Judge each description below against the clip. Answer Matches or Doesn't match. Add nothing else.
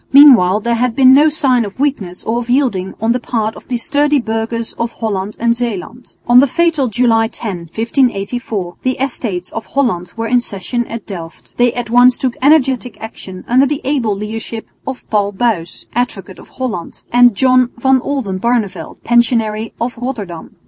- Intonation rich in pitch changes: Doesn't match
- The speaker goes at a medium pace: Matches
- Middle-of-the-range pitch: Doesn't match